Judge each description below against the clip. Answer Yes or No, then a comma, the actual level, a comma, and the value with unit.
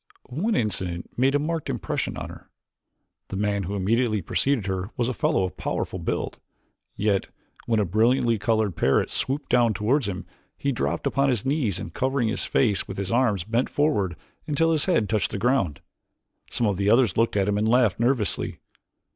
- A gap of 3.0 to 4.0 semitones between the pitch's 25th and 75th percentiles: No, average, 4.8 semitones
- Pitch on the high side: No, low, 110 Hz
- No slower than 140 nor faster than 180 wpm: No, average, 190 wpm